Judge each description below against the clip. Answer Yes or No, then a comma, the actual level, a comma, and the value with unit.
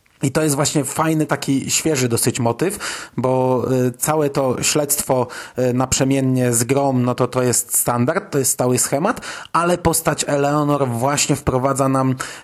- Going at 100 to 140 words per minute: No, average, 150 wpm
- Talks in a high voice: No, low, 135 Hz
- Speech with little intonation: No, average, 3.0 semitones